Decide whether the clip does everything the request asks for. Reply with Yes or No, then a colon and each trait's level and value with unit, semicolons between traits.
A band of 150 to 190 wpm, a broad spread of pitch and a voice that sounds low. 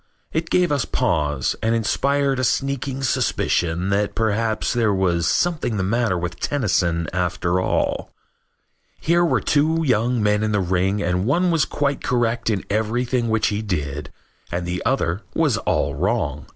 Yes: average, 160 wpm; wide, 6.2 semitones; low, 110 Hz